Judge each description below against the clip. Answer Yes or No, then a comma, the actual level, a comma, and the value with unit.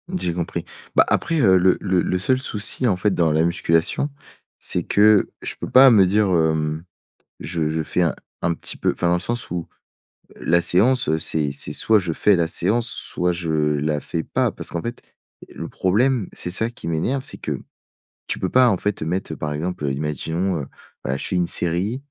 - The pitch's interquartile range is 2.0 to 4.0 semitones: No, average, 4.5 semitones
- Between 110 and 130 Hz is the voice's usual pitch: No, very low, 90 Hz